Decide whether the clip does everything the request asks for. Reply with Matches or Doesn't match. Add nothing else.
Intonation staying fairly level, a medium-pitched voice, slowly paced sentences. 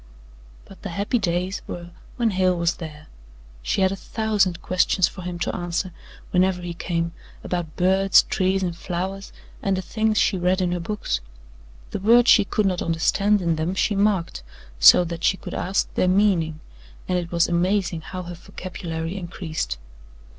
Doesn't match